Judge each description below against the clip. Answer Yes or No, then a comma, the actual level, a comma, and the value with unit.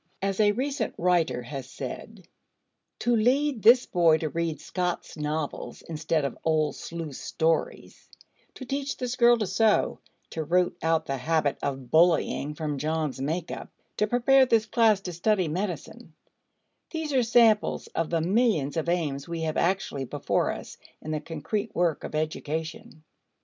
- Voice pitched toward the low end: No, medium, 170 Hz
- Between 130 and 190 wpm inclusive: Yes, average, 160 wpm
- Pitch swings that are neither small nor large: No, wide, 5.8 semitones